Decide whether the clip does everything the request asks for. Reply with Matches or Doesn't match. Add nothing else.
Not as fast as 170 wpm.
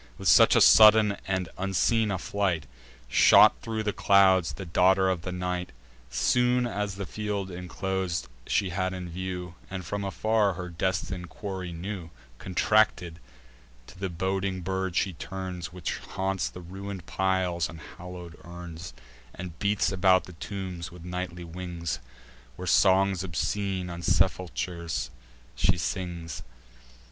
Matches